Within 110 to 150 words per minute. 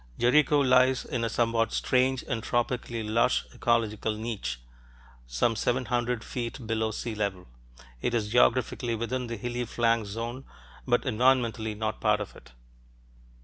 Yes: average, 145 wpm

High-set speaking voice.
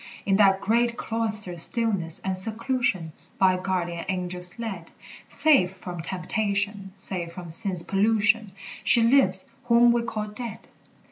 Yes: high, 195 Hz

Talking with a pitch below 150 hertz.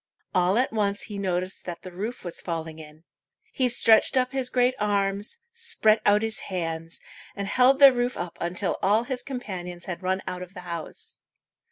No: high, 200 Hz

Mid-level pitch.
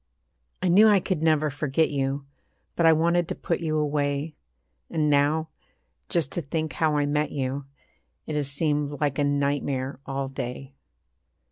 Yes: medium, 150 Hz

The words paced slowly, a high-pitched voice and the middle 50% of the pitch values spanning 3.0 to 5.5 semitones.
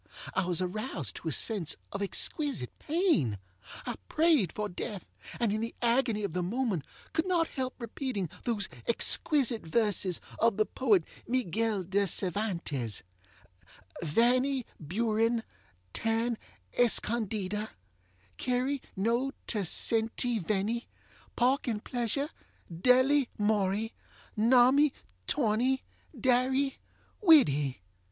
Yes: slow, 110 wpm; high, 225 Hz; average, 4.6 semitones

